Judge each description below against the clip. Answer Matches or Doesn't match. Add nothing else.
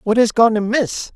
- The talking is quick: Matches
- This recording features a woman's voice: Matches